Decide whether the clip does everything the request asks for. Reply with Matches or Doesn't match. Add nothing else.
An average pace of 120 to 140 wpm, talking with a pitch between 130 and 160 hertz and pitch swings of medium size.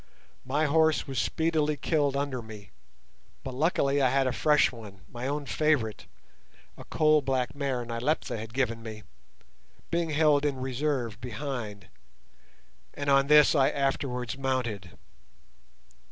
Matches